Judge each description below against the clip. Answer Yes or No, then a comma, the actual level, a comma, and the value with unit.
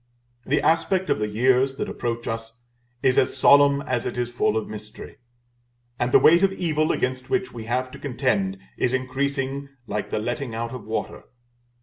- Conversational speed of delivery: Yes, average, 185 wpm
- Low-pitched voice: Yes, low, 130 Hz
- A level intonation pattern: No, average, 3.5 semitones